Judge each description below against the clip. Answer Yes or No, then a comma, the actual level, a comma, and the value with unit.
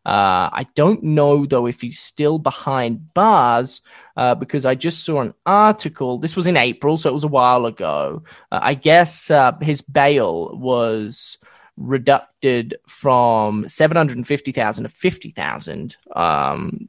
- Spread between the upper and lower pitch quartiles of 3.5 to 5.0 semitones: Yes, average, 4.5 semitones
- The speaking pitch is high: No, medium, 140 Hz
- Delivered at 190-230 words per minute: No, average, 165 wpm